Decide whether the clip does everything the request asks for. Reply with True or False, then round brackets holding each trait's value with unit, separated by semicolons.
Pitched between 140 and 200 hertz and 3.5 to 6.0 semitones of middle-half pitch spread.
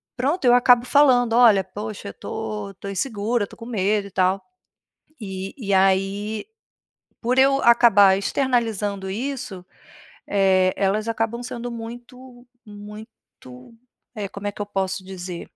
False (210 Hz; 3.8 semitones)